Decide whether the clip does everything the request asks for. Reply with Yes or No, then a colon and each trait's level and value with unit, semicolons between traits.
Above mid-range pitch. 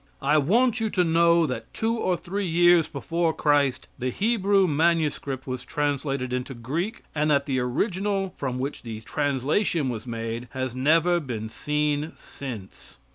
No: medium, 150 Hz